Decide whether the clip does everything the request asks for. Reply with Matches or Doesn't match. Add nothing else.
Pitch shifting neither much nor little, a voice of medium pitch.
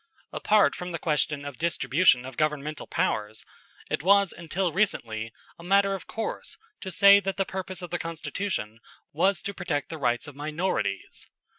Matches